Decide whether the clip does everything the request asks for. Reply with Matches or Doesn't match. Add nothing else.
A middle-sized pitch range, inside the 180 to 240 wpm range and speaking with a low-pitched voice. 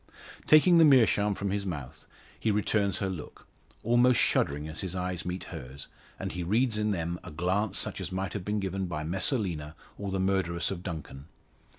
Matches